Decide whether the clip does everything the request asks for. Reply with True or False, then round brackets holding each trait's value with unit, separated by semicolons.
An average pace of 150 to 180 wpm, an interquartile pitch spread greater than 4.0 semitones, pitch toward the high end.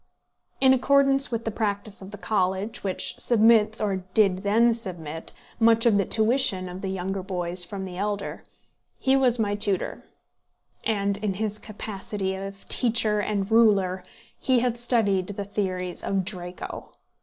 False (155 wpm; 2.9 semitones; 205 Hz)